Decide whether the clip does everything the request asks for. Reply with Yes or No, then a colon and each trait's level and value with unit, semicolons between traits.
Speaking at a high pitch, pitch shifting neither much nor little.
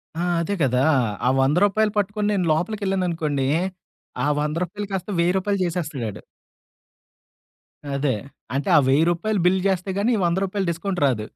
No: medium, 180 Hz; average, 5.0 semitones